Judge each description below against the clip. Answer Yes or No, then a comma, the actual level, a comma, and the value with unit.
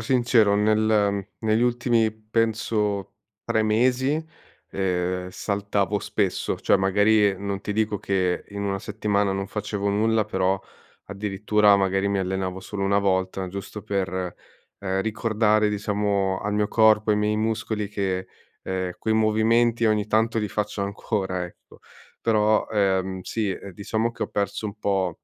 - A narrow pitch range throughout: Yes, narrow, 2.0 semitones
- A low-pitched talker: Yes, low, 105 Hz